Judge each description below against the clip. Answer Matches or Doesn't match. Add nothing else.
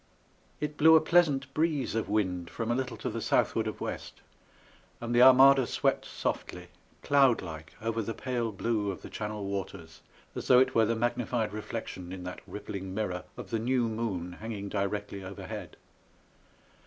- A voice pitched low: Matches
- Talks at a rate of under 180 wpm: Matches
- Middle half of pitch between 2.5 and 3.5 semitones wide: Doesn't match